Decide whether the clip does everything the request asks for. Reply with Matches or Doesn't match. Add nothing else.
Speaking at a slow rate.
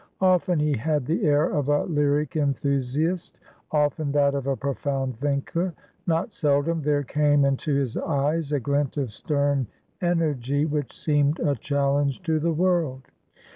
Doesn't match